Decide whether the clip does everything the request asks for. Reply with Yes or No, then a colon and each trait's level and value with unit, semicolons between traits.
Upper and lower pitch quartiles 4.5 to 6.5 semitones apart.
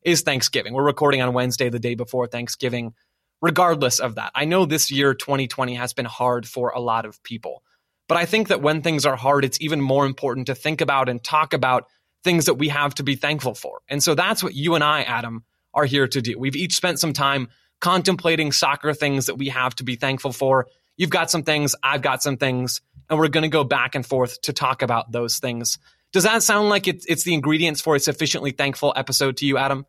No: average, 3.7 semitones